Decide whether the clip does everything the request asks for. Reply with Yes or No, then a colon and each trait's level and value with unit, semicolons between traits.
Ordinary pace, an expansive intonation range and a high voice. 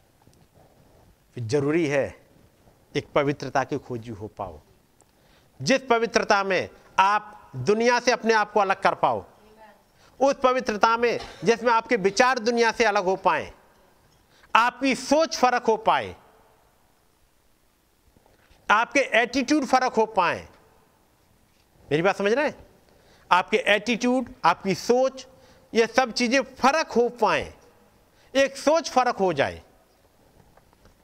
Yes: average, 120 wpm; wide, 6.0 semitones; high, 220 Hz